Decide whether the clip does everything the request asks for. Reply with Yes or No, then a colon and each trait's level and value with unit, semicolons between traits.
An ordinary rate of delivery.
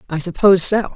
Yes: average, 190 wpm